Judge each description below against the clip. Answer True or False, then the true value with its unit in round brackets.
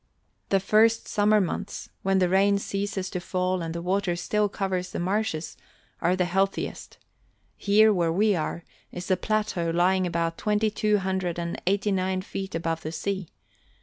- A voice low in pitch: False (190 Hz)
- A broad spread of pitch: False (2.4 semitones)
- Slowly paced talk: False (170 wpm)